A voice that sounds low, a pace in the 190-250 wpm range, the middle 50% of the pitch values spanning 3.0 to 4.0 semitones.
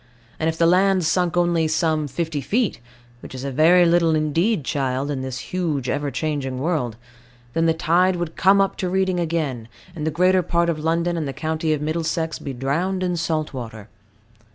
No: medium, 160 Hz; average, 195 wpm; average, 3.3 semitones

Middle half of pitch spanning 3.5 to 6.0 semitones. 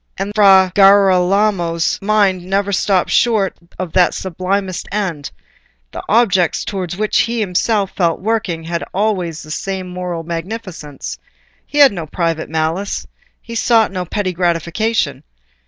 No: average, 3.1 semitones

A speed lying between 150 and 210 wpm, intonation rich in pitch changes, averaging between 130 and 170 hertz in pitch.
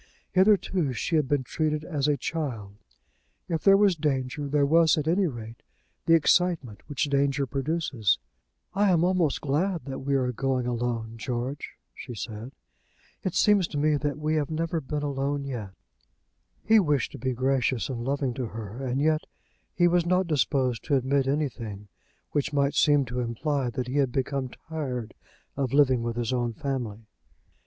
No: average, 170 wpm; average, 3.8 semitones; medium, 140 Hz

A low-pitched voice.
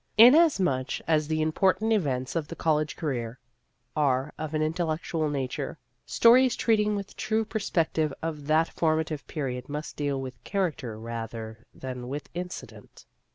No: medium, 155 Hz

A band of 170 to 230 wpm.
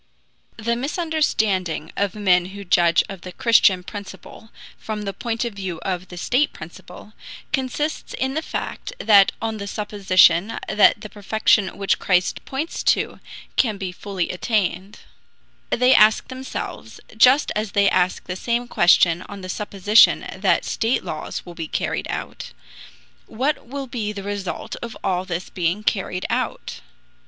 No: average, 150 wpm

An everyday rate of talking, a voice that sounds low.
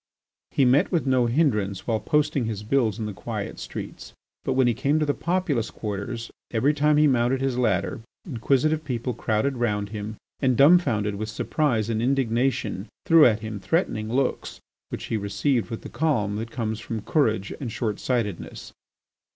Yes: average, 175 wpm; low, 120 Hz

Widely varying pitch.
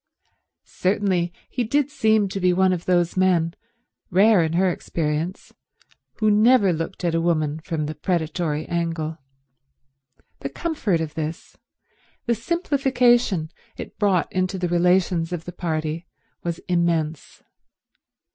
No: average, 3.5 semitones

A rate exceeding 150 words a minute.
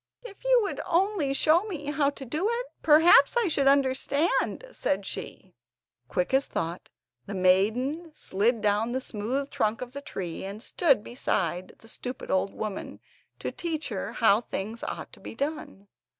Yes: average, 165 wpm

